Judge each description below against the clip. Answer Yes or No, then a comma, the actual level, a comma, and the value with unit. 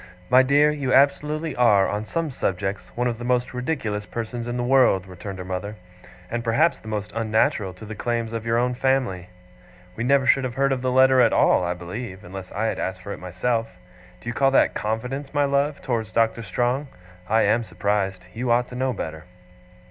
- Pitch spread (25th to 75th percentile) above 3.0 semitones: Yes, average, 4.0 semitones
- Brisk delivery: Yes, fast, 210 wpm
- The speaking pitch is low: Yes, low, 120 Hz